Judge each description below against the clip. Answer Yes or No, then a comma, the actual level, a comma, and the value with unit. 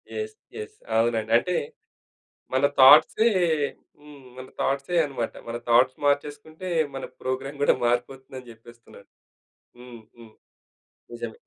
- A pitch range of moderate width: Yes, average, 3.8 semitones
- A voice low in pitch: Yes, low, 130 Hz